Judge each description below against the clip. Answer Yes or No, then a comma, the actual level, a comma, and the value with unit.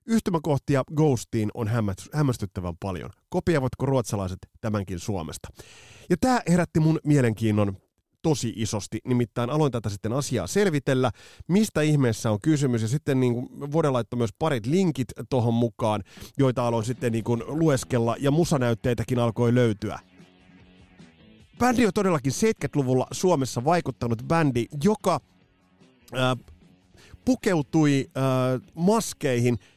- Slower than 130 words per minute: Yes, average, 115 wpm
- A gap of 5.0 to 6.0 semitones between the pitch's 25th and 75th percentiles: Yes, wide, 5.4 semitones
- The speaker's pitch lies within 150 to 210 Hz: No, low, 125 Hz